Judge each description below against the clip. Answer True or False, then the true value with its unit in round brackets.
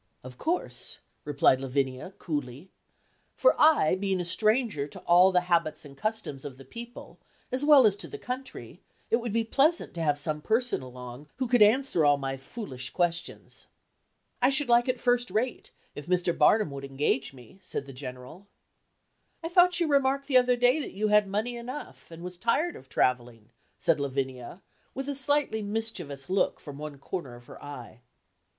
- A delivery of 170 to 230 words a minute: True (180 wpm)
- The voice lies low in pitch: False (185 Hz)